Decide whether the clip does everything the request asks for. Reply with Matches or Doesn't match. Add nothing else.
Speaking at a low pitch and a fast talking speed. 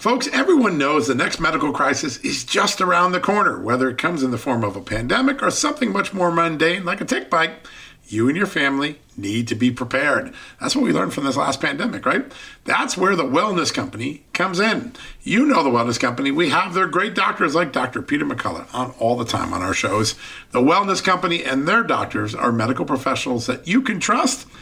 Doesn't match